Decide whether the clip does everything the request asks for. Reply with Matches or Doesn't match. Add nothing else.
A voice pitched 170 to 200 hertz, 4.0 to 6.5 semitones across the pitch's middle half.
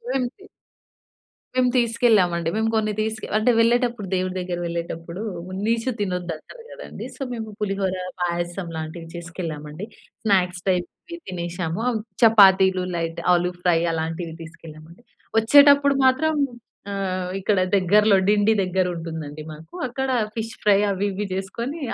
Matches